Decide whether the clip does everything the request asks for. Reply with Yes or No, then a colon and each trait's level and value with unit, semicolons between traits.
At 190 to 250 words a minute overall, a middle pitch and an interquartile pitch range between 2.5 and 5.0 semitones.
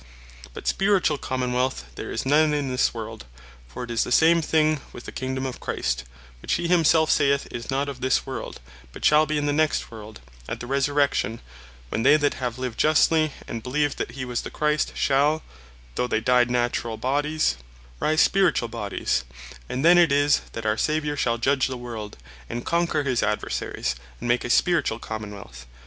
No: average, 195 wpm; low, 130 Hz; average, 4.2 semitones